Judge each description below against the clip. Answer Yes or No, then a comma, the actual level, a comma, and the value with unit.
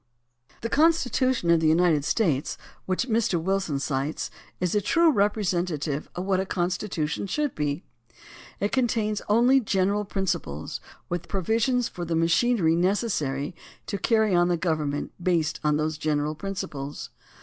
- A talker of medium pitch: Yes, medium, 180 Hz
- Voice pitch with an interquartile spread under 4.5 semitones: No, average, 5.3 semitones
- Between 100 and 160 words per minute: Yes, average, 150 wpm